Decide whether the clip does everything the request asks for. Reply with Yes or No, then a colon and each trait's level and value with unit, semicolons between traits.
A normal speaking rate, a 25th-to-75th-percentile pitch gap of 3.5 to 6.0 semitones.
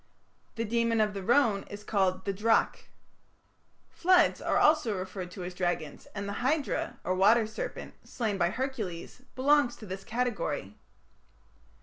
Yes: average, 145 wpm; average, 4.4 semitones